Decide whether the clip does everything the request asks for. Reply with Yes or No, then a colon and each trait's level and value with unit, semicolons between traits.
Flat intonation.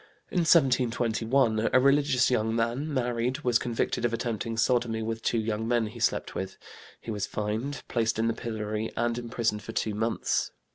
Yes: narrow, 1.9 semitones